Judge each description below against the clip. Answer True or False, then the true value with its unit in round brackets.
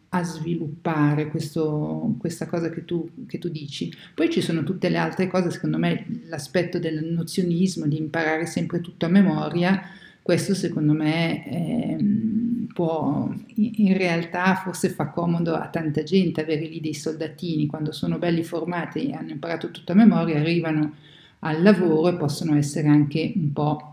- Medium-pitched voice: True (165 Hz)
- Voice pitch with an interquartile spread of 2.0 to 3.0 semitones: True (2.5 semitones)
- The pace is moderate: True (160 wpm)